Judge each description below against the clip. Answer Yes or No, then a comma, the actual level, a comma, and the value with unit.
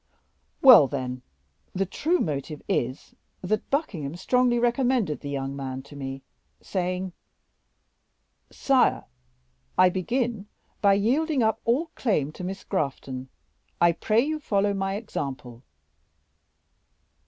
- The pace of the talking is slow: Yes, slow, 115 wpm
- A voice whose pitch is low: No, high, 190 Hz